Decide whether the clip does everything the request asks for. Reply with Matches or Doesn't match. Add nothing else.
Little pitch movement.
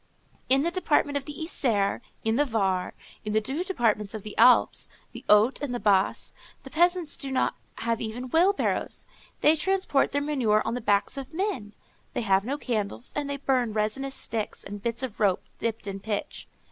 Doesn't match